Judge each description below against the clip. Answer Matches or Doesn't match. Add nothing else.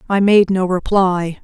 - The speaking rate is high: Doesn't match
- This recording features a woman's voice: Matches